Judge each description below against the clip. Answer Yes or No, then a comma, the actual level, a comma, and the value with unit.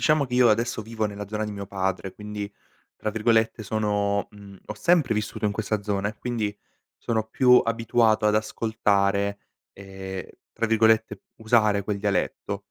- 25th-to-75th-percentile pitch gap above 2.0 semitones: No, narrow, 1.7 semitones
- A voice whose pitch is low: Yes, low, 105 Hz